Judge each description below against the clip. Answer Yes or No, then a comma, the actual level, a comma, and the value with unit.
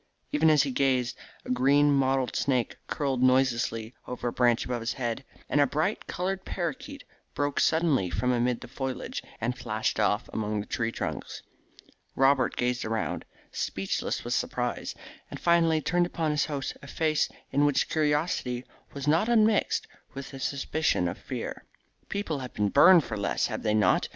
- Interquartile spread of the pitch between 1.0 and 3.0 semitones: No, average, 4.0 semitones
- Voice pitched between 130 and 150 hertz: Yes, low, 135 Hz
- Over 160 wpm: Yes, average, 170 wpm